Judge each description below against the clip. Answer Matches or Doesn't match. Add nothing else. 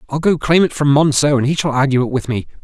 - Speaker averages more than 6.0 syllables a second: Matches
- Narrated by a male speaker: Matches